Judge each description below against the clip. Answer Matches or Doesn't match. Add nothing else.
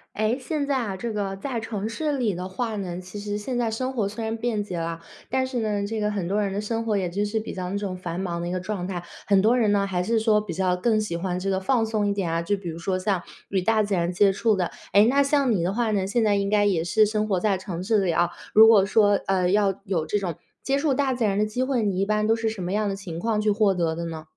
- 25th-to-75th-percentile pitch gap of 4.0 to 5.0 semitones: Doesn't match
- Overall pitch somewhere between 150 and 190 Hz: Doesn't match